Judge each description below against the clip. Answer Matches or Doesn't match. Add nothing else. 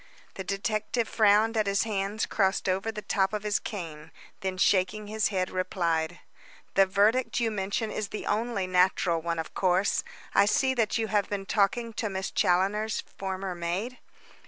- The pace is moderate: Matches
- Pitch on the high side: Matches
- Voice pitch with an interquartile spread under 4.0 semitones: Matches